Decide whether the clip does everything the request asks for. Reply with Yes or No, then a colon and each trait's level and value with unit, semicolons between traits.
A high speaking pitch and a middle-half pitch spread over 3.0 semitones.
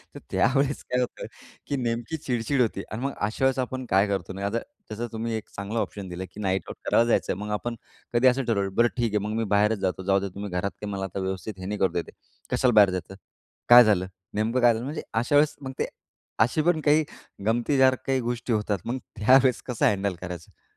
No: low, 110 Hz; average, 4.1 semitones